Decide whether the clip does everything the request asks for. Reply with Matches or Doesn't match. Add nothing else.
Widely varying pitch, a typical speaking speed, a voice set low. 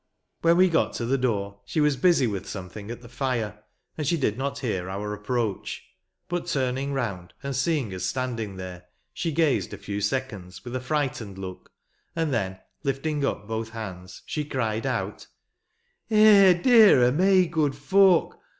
Matches